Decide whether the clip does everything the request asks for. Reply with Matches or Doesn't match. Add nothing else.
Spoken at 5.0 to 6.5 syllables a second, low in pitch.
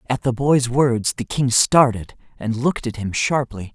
Doesn't match